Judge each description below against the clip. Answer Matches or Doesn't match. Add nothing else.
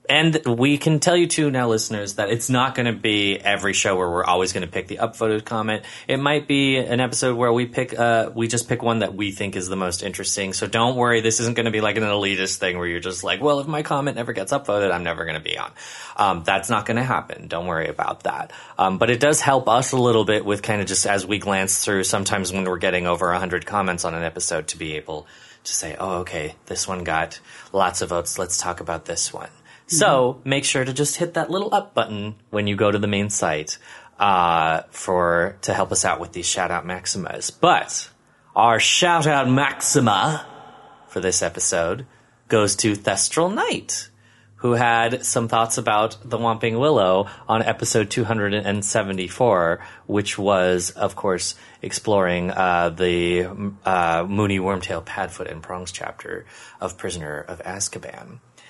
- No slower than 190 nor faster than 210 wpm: Matches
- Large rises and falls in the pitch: Doesn't match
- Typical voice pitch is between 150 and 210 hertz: Doesn't match